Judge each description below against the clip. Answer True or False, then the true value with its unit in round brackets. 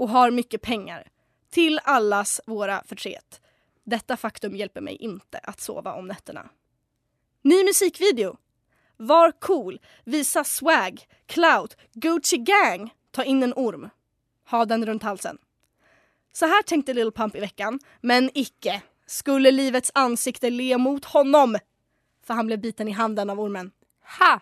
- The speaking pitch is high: True (250 Hz)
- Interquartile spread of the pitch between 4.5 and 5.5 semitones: True (5.2 semitones)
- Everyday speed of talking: True (145 wpm)